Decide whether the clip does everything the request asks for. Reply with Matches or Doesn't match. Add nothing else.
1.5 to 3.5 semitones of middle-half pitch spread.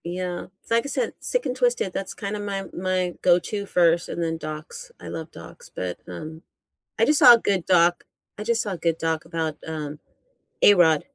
Doesn't match